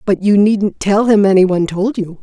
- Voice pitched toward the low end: No, high, 200 Hz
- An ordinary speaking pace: No, fast, 245 wpm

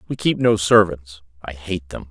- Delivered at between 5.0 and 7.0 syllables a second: No, 4.7 syllables/s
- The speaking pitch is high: No, very low, 90 Hz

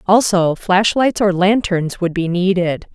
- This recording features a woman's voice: Yes, female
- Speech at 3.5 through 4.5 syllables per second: Yes, 4.0 syllables/s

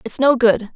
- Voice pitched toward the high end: Yes, high, 235 Hz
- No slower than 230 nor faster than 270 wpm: Yes, fast, 235 wpm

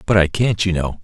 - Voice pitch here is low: Yes, very low, 90 Hz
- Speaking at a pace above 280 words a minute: Yes, fast, 290 wpm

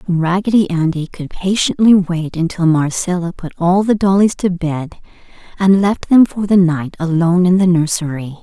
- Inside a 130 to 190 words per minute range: Yes, average, 165 wpm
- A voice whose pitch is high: No, medium, 180 Hz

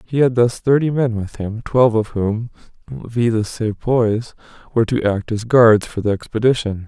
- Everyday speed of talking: Yes, average, 185 wpm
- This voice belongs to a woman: No, male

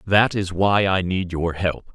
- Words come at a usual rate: No, fast, 215 wpm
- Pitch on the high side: No, very low, 95 Hz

